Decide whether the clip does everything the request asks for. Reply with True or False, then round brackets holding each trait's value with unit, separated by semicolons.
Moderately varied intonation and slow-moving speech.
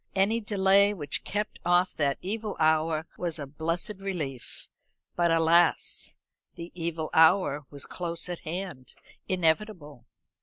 True (3.4 semitones; 125 wpm)